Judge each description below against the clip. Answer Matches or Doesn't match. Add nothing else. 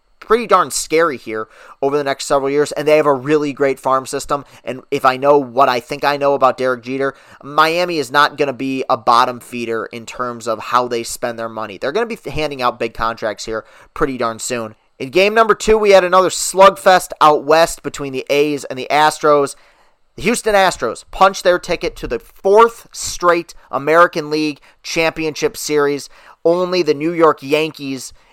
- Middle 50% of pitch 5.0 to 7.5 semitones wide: Doesn't match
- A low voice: Doesn't match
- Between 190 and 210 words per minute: Matches